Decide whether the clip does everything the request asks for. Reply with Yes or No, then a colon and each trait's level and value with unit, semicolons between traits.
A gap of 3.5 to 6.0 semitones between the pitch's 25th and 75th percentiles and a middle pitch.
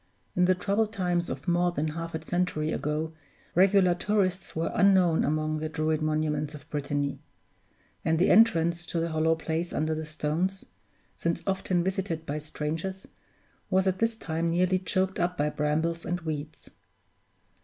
No: average, 3.0 semitones; medium, 165 Hz